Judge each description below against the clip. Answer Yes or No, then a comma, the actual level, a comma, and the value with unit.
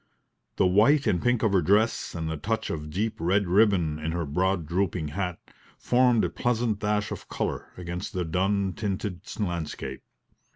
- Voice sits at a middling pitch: No, very low, 95 Hz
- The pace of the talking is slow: No, average, 170 wpm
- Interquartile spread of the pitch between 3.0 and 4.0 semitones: Yes, average, 3.7 semitones